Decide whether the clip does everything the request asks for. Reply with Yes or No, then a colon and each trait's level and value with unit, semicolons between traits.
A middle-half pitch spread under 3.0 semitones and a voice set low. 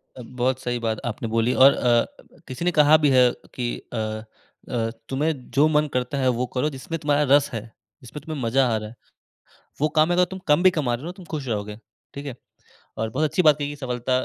No: average, 3.8 semitones; low, 130 Hz